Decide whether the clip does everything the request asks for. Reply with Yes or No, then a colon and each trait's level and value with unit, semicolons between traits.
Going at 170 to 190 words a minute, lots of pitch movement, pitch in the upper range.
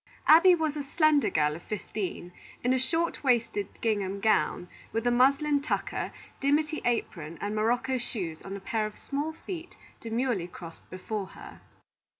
No: average, 155 wpm; wide, 6.5 semitones; high, 235 Hz